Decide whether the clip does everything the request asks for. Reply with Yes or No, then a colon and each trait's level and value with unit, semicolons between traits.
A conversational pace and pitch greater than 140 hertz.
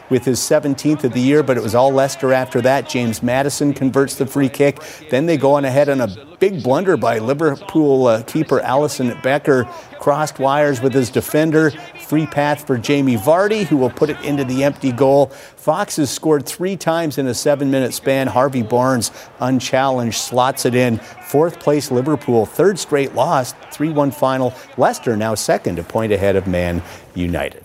No: average, 180 wpm; low, 135 Hz